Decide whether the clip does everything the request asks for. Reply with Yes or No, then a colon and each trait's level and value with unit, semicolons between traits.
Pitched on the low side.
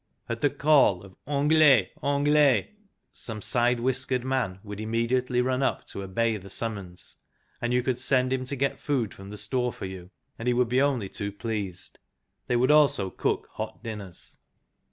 Yes: low, 120 Hz